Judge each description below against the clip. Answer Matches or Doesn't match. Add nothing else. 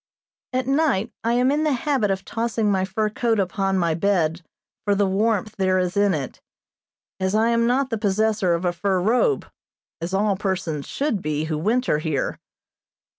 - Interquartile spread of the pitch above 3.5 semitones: Matches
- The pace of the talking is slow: Doesn't match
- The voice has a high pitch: Matches